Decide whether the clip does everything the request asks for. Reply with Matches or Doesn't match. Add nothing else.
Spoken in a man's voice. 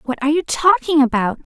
Doesn't match